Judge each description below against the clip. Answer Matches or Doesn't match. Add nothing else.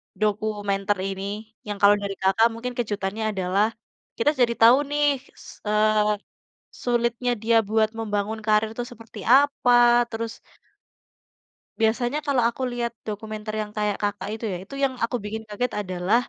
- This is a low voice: Doesn't match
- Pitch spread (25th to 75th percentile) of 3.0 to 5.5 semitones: Doesn't match